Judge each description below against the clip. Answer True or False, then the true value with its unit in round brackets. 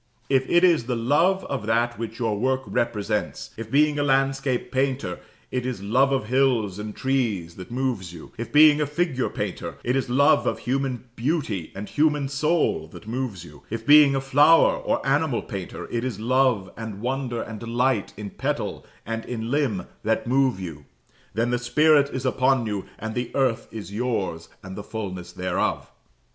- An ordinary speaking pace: True (180 wpm)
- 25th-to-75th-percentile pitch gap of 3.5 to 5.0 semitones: True (4.1 semitones)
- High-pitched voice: False (125 Hz)